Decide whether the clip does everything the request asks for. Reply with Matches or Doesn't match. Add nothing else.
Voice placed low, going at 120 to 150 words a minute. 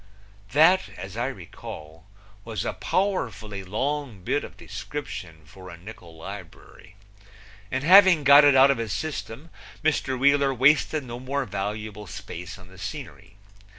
Matches